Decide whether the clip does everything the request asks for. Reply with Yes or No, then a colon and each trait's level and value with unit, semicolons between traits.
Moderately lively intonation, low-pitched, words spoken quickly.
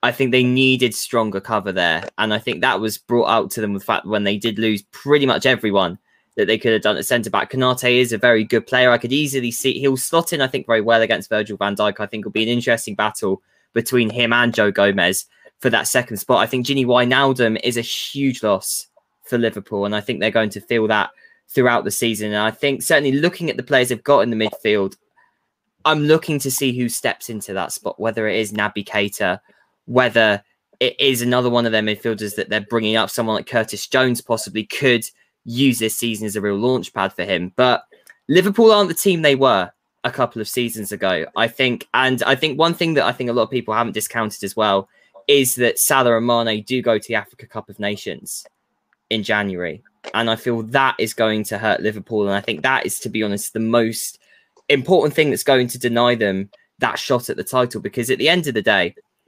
Yes: average, 3.3 semitones; low, 115 Hz; fast, 235 wpm